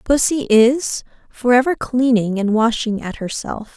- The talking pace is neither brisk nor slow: Yes, average, 145 wpm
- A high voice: Yes, high, 235 Hz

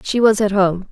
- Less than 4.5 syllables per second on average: No, 4.9 syllables/s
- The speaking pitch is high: Yes, high, 200 Hz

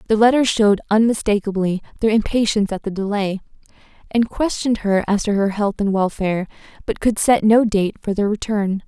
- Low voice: No, high, 210 Hz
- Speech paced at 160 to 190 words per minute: Yes, average, 175 wpm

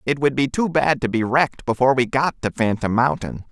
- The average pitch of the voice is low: Yes, low, 130 Hz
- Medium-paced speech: No, fast, 240 wpm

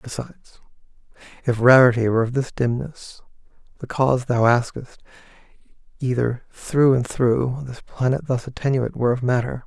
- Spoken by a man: Yes, male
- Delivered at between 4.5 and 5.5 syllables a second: Yes, 5.2 syllables/s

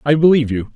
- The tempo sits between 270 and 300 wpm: No, fast, 240 wpm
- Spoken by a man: Yes, male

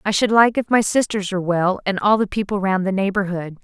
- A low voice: No, high, 195 Hz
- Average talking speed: No, fast, 250 wpm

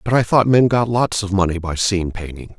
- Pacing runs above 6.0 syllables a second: No, 5.6 syllables/s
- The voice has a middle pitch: No, low, 100 Hz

